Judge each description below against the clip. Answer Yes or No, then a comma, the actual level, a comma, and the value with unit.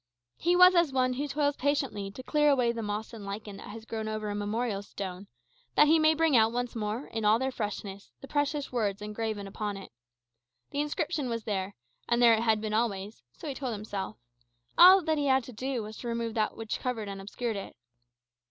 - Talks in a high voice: Yes, high, 230 Hz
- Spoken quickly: Yes, fast, 215 wpm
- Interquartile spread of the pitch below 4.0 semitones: No, average, 4.6 semitones